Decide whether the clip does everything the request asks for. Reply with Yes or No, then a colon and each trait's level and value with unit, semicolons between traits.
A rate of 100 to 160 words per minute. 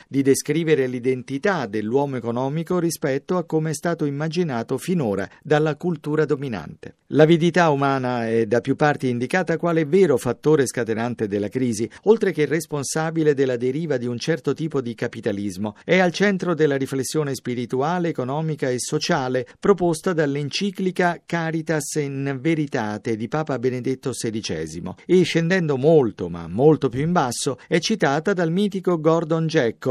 Yes: average, 140 wpm